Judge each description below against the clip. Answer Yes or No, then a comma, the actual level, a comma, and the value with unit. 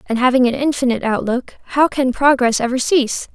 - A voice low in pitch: No, very high, 255 Hz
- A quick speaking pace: No, average, 180 wpm